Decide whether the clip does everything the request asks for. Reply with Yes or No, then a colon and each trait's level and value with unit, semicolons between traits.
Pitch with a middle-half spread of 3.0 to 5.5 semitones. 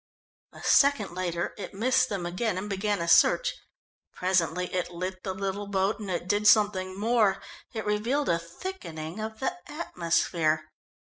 Yes: average, 3.5 semitones